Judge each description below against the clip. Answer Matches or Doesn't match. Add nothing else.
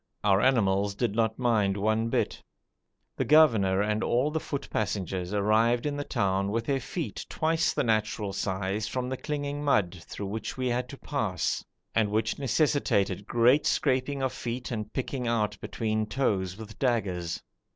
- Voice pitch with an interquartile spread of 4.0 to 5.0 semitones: Matches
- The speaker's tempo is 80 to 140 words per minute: Doesn't match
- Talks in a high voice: Doesn't match